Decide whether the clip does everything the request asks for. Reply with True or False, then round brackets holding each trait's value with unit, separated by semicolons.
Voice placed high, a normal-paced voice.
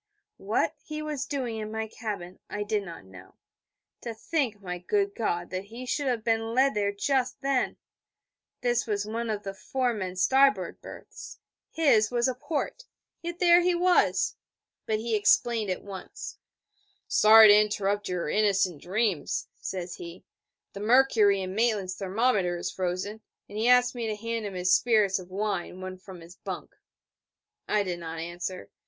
True (215 Hz; 170 wpm)